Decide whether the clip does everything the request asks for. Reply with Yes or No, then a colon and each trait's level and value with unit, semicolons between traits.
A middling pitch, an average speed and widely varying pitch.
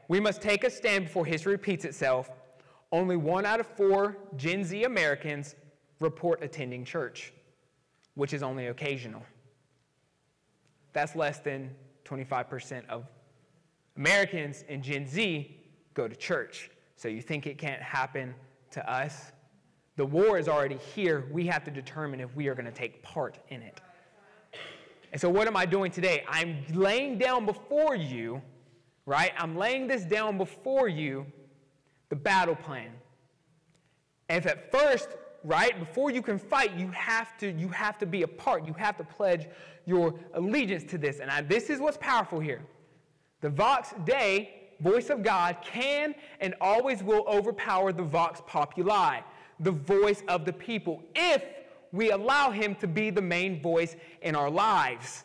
Yes: medium, 170 Hz; average, 160 wpm; wide, 6.0 semitones